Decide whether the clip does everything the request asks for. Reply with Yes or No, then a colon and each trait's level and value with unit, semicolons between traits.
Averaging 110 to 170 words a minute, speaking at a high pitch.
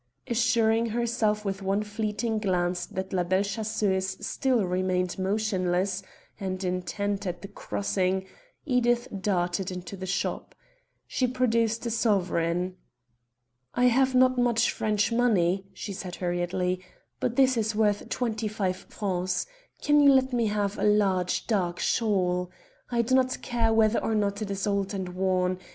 Yes: average, 150 wpm; high, 205 Hz